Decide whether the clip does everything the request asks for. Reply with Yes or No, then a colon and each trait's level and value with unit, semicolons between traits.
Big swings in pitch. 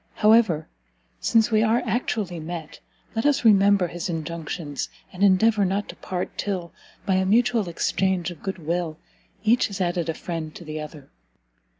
No: average, 4.2 semitones